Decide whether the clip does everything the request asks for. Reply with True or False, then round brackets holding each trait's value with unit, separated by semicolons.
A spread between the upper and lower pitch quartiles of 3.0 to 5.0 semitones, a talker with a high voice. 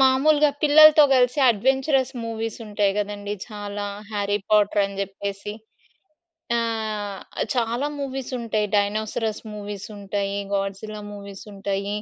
True (3.3 semitones; 210 Hz)